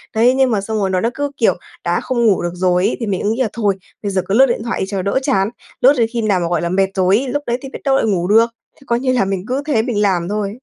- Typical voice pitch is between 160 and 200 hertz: No, high, 215 Hz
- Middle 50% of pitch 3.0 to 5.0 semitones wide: Yes, average, 4.3 semitones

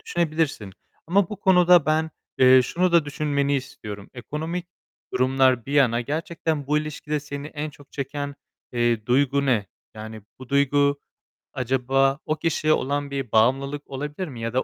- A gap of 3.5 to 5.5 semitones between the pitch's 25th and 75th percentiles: No, average, 2.9 semitones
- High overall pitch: No, medium, 140 Hz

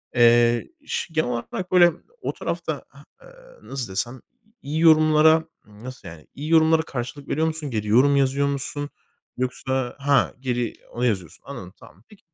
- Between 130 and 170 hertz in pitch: Yes, low, 135 Hz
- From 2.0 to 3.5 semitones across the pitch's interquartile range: No, average, 4.7 semitones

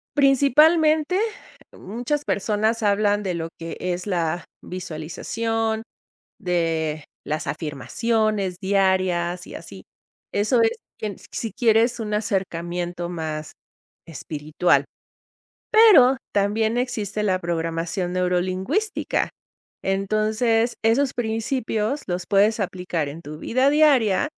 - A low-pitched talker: No, high, 205 Hz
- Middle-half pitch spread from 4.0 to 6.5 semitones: Yes, average, 4.6 semitones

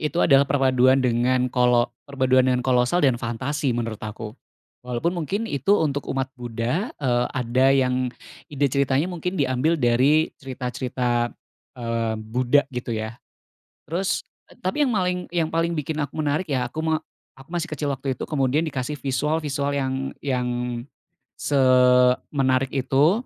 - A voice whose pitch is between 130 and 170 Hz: Yes, low, 135 Hz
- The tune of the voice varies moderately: Yes, average, 3.2 semitones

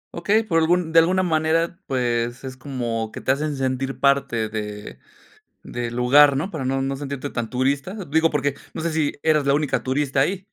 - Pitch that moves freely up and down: No, average, 3.8 semitones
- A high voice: No, medium, 140 Hz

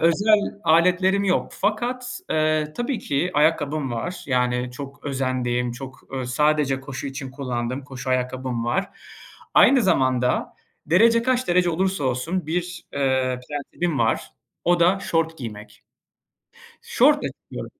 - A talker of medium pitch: Yes, medium, 145 Hz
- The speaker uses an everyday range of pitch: No, wide, 5.8 semitones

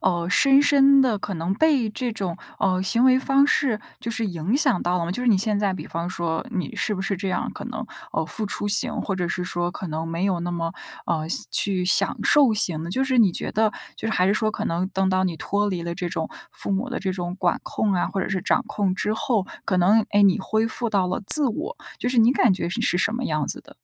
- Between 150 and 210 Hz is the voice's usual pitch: Yes, high, 195 Hz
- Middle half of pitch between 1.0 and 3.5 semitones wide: No, average, 4.3 semitones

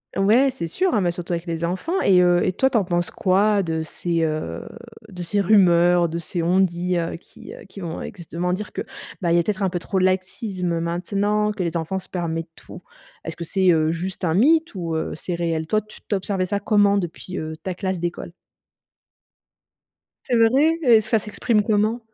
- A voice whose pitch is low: No, medium, 185 Hz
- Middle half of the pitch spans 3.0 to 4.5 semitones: Yes, average, 3.4 semitones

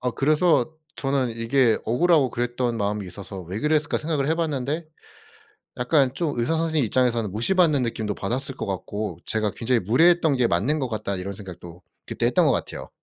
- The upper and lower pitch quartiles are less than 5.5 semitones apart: No, wide, 6.0 semitones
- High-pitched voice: No, low, 125 Hz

